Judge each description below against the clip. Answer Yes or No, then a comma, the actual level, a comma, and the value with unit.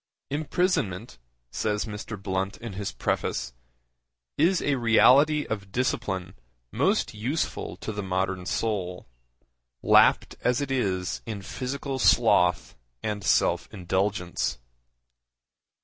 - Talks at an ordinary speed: No, slow, 105 wpm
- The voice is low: Yes, low, 105 Hz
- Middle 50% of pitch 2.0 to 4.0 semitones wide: No, average, 5.2 semitones